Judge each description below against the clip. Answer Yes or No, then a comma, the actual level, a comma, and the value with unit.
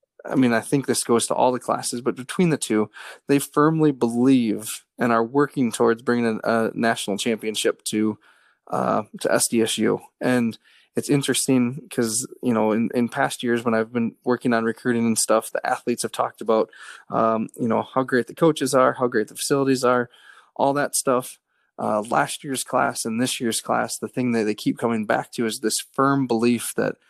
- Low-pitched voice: Yes, low, 120 Hz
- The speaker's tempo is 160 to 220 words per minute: Yes, average, 200 wpm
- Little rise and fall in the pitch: Yes, narrow, 2.3 semitones